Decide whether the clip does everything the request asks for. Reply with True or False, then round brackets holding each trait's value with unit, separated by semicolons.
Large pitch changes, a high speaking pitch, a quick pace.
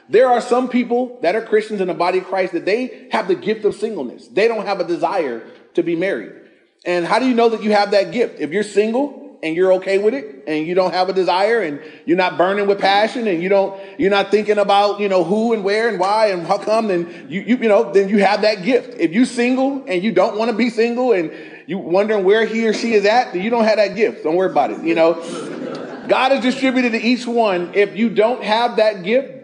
False (4.0 semitones; 210 Hz; 260 wpm)